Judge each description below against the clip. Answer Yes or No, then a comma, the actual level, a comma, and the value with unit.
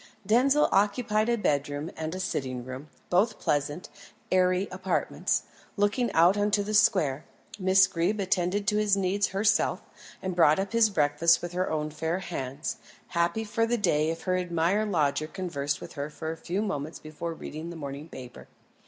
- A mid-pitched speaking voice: Yes, medium, 180 Hz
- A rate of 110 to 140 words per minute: No, average, 170 wpm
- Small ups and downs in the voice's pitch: No, average, 4.8 semitones